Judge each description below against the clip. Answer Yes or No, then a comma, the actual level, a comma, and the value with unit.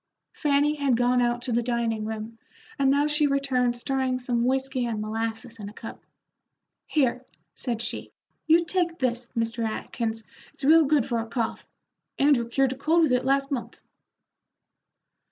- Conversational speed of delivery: Yes, average, 165 wpm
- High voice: Yes, very high, 250 Hz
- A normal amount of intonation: Yes, average, 3.1 semitones